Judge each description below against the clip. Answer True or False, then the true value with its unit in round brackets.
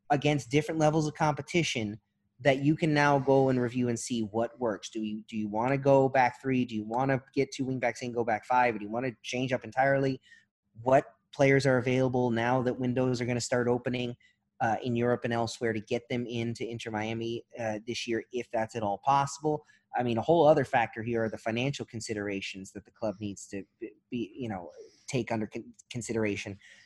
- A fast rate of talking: True (220 wpm)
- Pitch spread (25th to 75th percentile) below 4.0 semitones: True (3.1 semitones)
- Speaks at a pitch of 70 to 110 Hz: False (120 Hz)